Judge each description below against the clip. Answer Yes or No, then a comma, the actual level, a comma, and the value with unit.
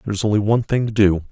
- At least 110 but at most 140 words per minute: No, fast, 320 wpm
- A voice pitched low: Yes, low, 105 Hz